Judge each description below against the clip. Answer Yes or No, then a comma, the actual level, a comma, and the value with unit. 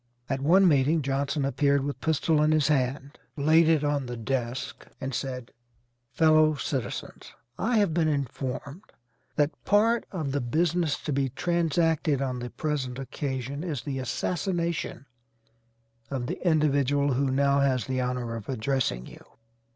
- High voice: No, medium, 140 Hz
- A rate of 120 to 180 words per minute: Yes, average, 150 wpm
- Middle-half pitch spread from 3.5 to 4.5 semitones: No, average, 3.1 semitones